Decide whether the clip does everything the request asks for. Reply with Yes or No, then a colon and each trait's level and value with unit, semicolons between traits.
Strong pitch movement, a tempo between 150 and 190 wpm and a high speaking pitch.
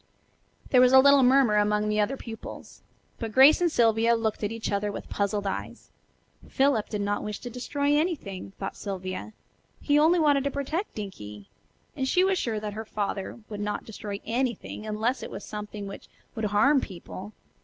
No: average, 4.5 semitones; average, 185 wpm; high, 220 Hz